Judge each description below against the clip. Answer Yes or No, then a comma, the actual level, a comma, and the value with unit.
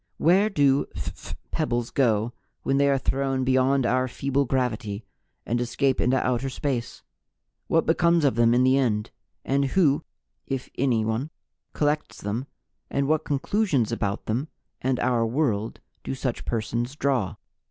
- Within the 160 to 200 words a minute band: No, average, 145 wpm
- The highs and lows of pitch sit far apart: No, average, 2.8 semitones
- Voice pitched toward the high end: No, low, 130 Hz